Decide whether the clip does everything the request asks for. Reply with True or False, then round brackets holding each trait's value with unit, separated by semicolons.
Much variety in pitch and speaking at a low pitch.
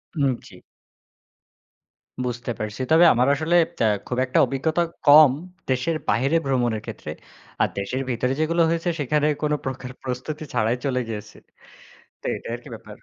False (3.8 semitones; 130 Hz)